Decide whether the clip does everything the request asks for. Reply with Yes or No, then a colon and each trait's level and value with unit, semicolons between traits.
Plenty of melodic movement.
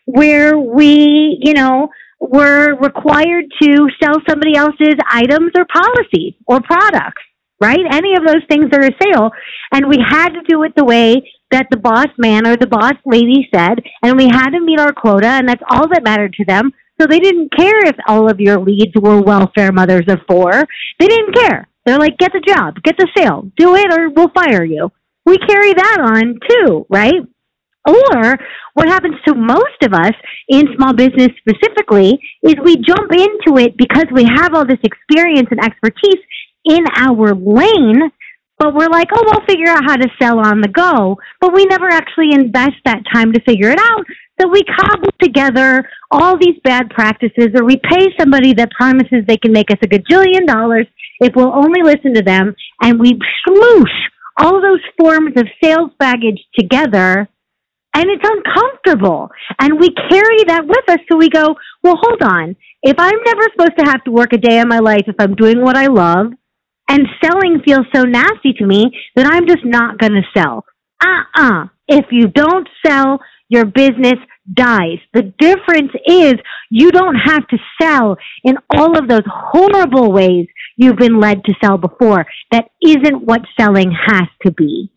Yes: wide, 6.3 semitones